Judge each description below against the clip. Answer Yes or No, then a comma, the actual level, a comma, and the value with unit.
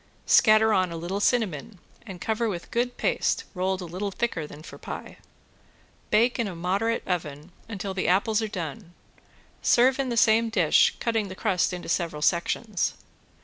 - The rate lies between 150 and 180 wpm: Yes, average, 170 wpm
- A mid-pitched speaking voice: No, high, 195 Hz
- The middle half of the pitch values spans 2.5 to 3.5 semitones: No, average, 4.2 semitones